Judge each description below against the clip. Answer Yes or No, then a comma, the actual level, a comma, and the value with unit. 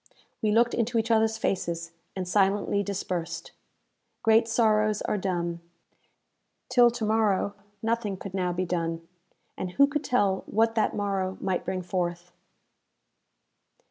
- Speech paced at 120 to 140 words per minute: Yes, slow, 135 wpm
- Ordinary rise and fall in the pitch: Yes, average, 3.6 semitones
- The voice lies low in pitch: No, high, 200 Hz